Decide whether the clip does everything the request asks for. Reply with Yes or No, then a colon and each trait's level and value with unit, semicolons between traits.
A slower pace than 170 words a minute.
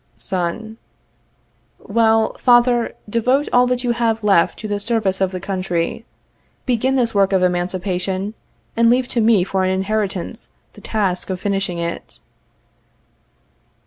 Yes: average, 140 wpm